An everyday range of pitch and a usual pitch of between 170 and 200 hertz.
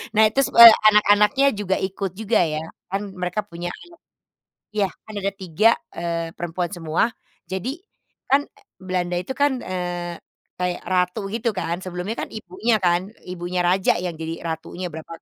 Yes: average, 3.5 semitones; medium, 185 Hz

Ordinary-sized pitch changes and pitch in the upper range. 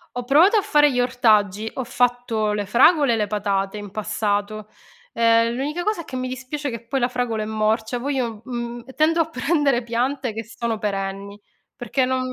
Yes: average, 3.6 semitones; high, 240 Hz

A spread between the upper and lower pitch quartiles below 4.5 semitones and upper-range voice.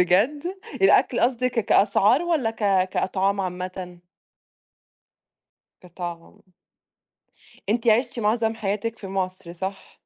Yes: average, 3.7 semitones; high, 200 Hz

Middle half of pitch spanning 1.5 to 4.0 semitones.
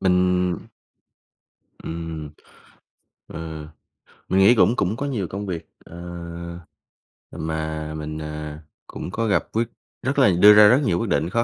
No: average, 4.7 semitones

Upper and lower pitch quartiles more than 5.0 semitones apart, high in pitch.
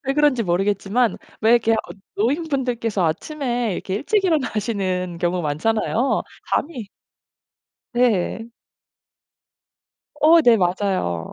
Yes: wide, 5.5 semitones; high, 225 Hz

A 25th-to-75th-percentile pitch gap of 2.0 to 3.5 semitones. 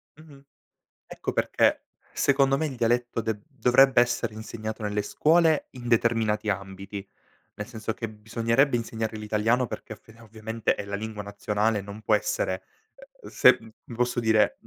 Yes: narrow, 2.4 semitones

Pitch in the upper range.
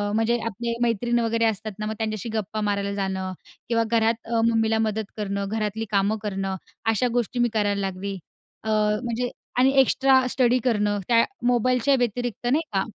Yes: high, 220 Hz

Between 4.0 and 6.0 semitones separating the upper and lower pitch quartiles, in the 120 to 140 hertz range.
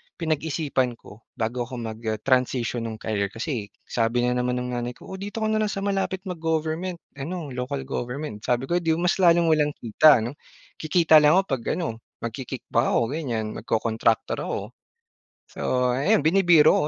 Yes: wide, 5.5 semitones; low, 135 Hz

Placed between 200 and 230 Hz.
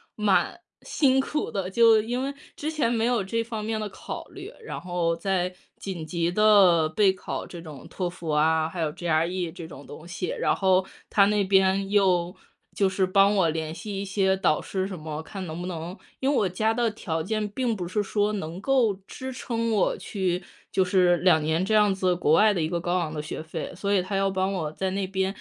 No: high, 190 Hz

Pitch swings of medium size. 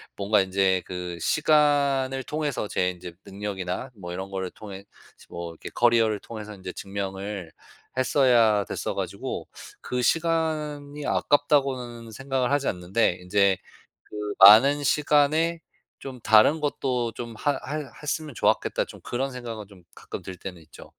No: wide, 6.6 semitones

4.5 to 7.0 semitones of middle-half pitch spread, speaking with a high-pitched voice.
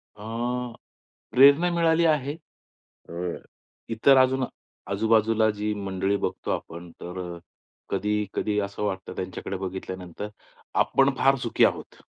No: average, 5.2 semitones; low, 105 Hz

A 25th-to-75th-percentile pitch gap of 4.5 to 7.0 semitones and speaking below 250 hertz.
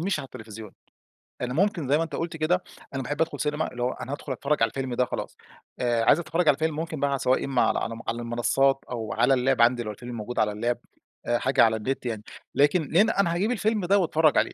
Yes: average, 5.2 semitones; low, 135 Hz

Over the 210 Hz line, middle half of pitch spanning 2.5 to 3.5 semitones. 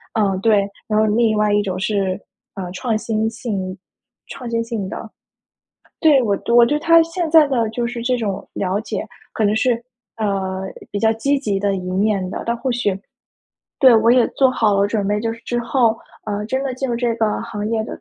Yes: high, 220 Hz; average, 2.9 semitones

